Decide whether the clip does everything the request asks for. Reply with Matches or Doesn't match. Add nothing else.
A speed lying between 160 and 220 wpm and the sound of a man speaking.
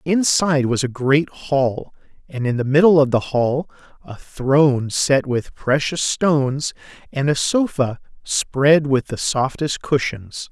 Doesn't match